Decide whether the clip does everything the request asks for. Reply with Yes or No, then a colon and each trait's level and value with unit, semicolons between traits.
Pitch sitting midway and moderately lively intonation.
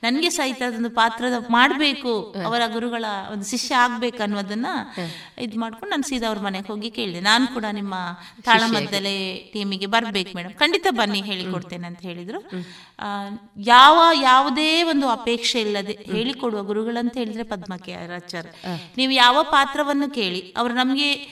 No: high, 230 Hz; average, 4.0 semitones